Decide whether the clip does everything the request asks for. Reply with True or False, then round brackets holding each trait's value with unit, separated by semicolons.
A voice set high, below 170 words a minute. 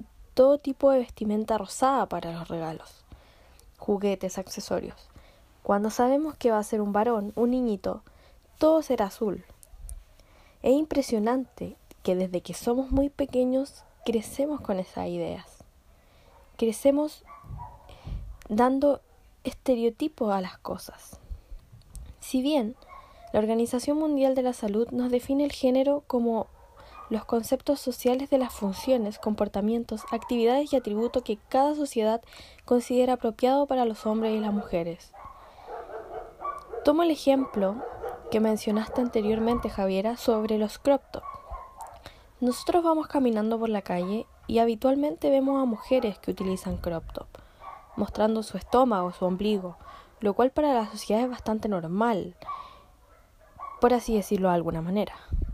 True (235 Hz; 130 wpm)